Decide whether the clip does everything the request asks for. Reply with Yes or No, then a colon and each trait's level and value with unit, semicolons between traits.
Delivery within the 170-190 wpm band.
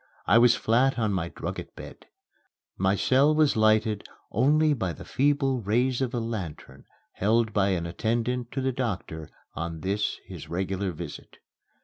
No: average, 155 wpm